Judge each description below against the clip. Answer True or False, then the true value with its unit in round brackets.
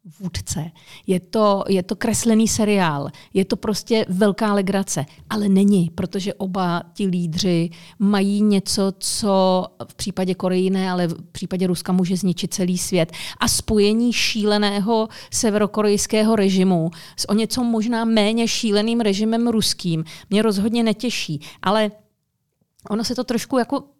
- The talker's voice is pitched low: False (200 Hz)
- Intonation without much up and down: False (3.1 semitones)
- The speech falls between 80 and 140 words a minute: True (135 wpm)